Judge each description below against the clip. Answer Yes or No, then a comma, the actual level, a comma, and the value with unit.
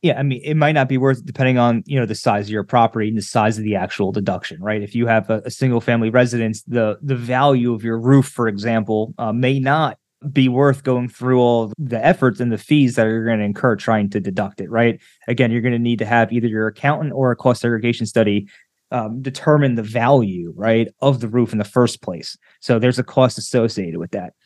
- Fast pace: Yes, fast, 245 wpm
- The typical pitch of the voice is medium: No, low, 120 Hz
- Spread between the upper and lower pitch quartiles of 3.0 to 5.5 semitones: No, narrow, 2.6 semitones